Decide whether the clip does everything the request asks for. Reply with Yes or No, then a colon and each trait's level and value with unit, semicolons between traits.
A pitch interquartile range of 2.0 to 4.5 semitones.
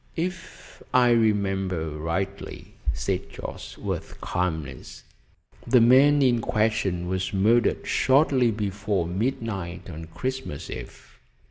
No: wide, 5.5 semitones